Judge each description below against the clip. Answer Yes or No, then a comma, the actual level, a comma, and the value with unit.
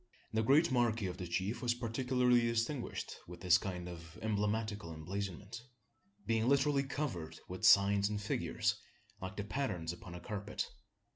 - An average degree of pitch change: Yes, average, 4.7 semitones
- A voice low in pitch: Yes, low, 105 Hz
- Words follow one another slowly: No, average, 150 wpm